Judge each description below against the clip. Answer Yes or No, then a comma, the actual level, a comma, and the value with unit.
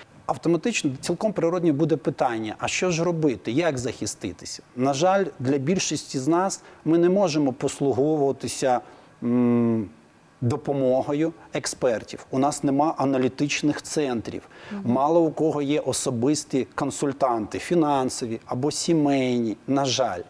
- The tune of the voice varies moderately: Yes, average, 4.0 semitones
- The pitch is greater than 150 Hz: No, medium, 145 Hz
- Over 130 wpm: No, average, 115 wpm